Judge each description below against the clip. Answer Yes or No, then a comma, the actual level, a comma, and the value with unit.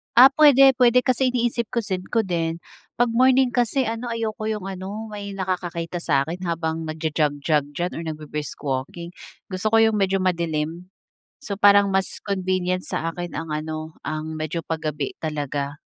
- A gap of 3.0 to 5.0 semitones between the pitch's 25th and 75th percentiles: No, wide, 5.5 semitones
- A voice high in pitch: No, medium, 180 Hz